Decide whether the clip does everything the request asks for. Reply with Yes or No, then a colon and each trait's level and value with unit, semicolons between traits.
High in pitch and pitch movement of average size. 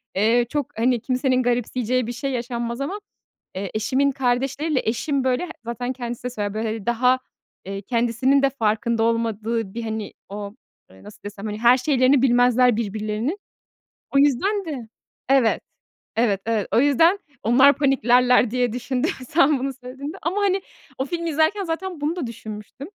Yes: high, 245 Hz; average, 3.4 semitones